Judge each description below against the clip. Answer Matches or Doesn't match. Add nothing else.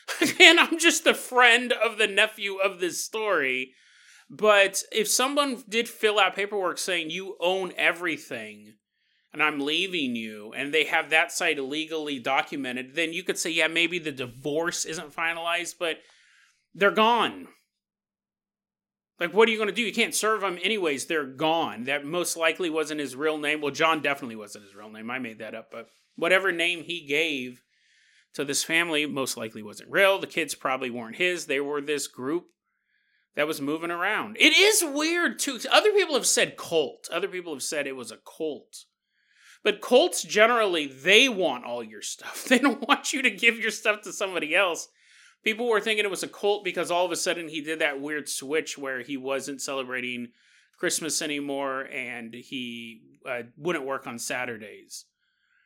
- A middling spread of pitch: Doesn't match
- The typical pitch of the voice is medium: Matches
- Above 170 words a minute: Matches